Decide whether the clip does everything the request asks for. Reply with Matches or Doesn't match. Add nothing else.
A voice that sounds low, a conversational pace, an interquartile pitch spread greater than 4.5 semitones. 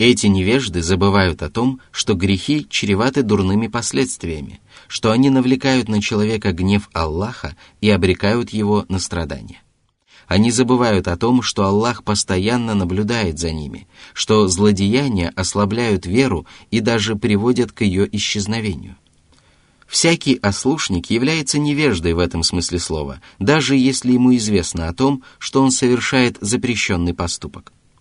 Matches